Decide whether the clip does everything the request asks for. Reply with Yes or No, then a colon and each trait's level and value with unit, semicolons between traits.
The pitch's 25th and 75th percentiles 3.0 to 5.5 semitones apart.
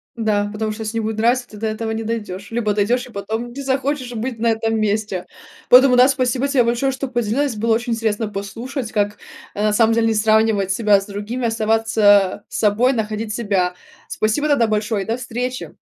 No: narrow, 2.5 semitones